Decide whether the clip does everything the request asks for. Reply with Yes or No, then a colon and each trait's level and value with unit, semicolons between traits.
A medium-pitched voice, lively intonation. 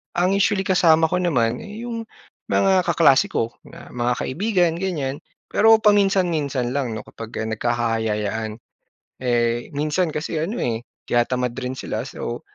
Yes: medium, 145 Hz; wide, 7.6 semitones